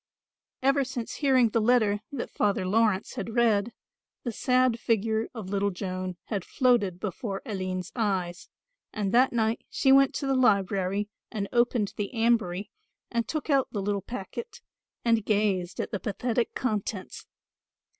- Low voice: No, high, 220 Hz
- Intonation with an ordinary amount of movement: Yes, average, 3.5 semitones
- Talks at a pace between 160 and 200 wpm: No, average, 150 wpm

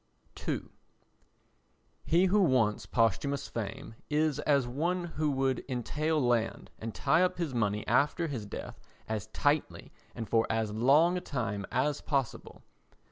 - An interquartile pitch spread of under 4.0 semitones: No, wide, 5.4 semitones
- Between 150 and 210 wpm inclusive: No, average, 140 wpm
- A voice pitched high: No, low, 135 Hz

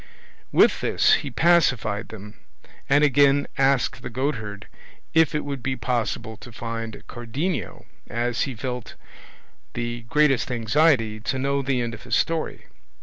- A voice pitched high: No, low, 125 Hz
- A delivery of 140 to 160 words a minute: Yes, average, 145 wpm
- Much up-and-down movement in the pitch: No, average, 3.7 semitones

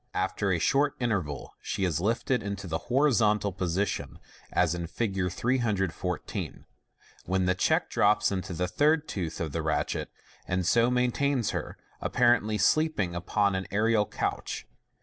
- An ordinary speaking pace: Yes, average, 150 wpm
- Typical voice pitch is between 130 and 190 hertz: No, low, 100 Hz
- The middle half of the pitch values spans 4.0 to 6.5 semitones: Yes, average, 4.9 semitones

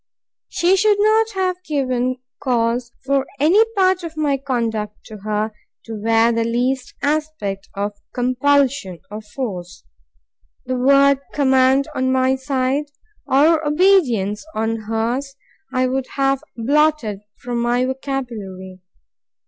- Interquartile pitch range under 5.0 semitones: Yes, average, 4.0 semitones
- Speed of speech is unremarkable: No, slow, 125 wpm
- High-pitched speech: Yes, very high, 260 Hz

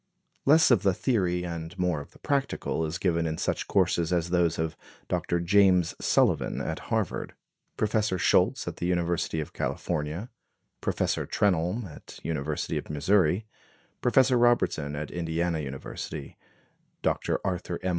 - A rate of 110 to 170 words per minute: Yes, average, 145 wpm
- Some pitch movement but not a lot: Yes, average, 3.4 semitones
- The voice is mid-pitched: No, very low, 85 Hz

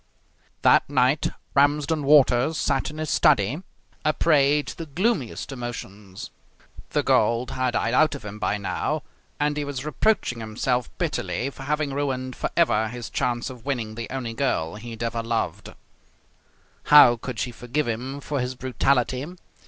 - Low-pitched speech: Yes, low, 130 Hz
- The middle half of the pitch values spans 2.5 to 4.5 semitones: Yes, average, 3.6 semitones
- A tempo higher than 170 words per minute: No, average, 160 wpm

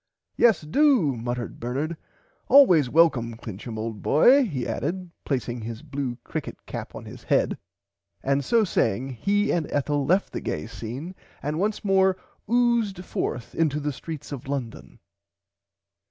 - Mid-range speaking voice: Yes, medium, 145 Hz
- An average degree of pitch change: No, wide, 7.6 semitones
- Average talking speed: Yes, average, 145 wpm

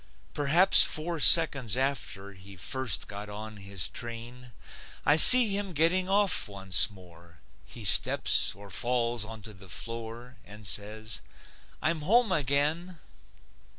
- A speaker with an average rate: No, slow, 125 wpm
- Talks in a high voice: No, low, 120 Hz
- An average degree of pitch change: No, wide, 7.4 semitones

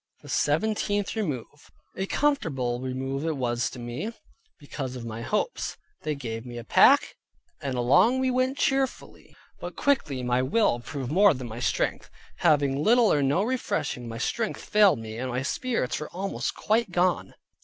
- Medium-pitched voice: Yes, medium, 145 Hz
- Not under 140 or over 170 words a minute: Yes, average, 165 wpm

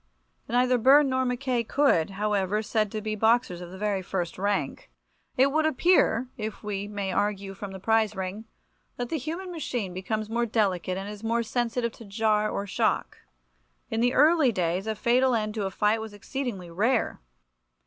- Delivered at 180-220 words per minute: Yes, average, 190 wpm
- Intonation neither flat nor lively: Yes, average, 3.8 semitones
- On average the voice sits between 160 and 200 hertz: No, high, 215 Hz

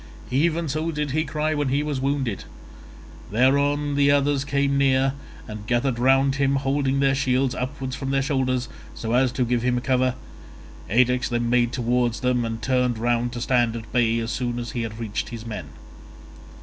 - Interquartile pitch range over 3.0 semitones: No, narrow, 2.5 semitones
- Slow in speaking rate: No, average, 185 wpm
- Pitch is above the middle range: No, low, 130 Hz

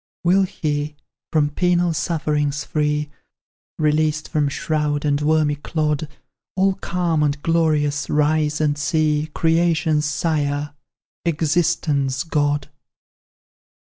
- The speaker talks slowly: Yes, slow, 100 wpm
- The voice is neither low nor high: Yes, medium, 150 Hz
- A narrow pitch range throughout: Yes, narrow, 1.6 semitones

